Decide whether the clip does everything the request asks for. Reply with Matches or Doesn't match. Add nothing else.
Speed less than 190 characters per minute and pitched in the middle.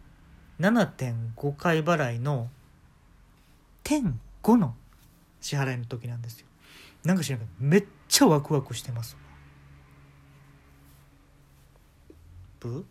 Doesn't match